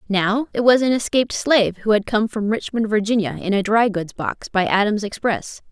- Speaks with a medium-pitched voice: No, high, 215 Hz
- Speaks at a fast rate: Yes, fast, 210 wpm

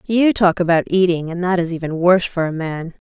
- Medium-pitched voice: Yes, medium, 175 Hz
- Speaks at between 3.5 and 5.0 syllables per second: No, 5.7 syllables/s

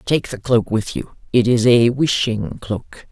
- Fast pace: No, average, 195 wpm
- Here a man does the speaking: Yes, male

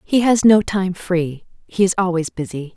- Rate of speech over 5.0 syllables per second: No, 4.6 syllables/s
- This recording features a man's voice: No, female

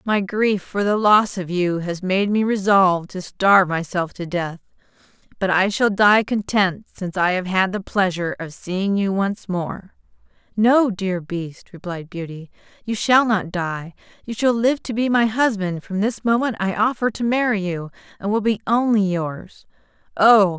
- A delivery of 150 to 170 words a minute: No, average, 180 wpm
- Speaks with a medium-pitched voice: No, high, 200 Hz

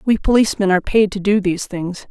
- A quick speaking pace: Yes, fast, 230 wpm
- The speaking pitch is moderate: No, high, 195 Hz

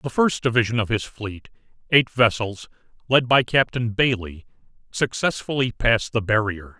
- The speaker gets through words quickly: No, average, 140 wpm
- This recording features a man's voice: Yes, male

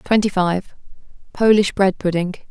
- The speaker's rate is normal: No, slow, 95 wpm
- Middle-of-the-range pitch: No, high, 195 Hz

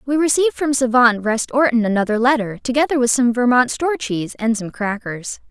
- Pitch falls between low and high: No, high, 245 Hz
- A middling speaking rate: Yes, average, 185 wpm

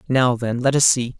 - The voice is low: Yes, low, 125 Hz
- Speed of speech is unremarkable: No, fast, 250 wpm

